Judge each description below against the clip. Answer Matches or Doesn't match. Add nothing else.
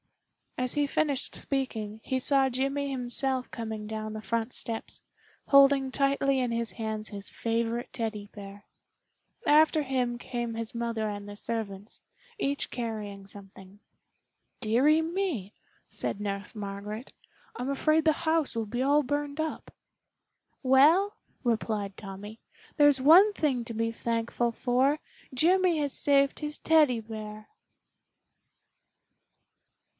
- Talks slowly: Matches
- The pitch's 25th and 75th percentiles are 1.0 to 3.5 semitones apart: Doesn't match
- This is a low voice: Doesn't match